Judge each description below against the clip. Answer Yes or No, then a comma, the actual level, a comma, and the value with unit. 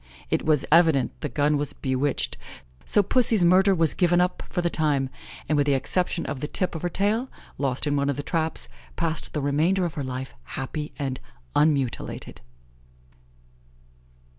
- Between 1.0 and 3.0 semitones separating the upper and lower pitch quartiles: No, average, 3.9 semitones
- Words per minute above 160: Yes, average, 170 wpm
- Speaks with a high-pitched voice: No, medium, 155 Hz